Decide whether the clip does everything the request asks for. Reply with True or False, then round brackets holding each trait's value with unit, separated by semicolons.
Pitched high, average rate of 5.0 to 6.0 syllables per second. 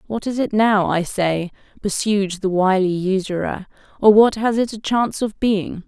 False (200 Hz; 4.4 syllables/s)